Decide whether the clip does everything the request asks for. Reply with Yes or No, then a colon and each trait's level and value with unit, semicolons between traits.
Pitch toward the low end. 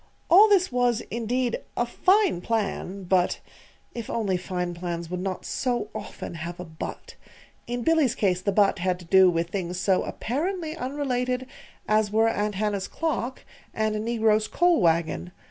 No: high, 215 Hz